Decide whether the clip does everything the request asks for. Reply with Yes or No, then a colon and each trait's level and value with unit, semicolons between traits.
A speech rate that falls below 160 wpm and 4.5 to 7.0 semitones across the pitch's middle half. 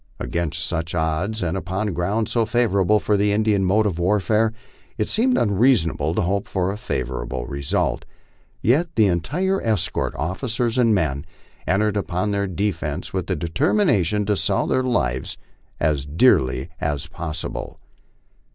Yes: average, 150 wpm; average, 5.0 semitones